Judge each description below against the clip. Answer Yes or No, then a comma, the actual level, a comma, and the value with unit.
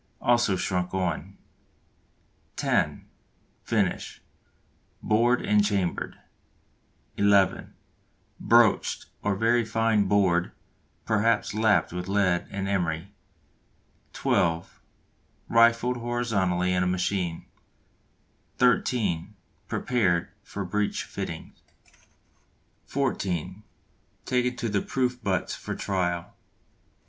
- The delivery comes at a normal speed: No, slow, 85 wpm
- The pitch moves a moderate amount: Yes, average, 4.2 semitones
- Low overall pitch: Yes, low, 100 Hz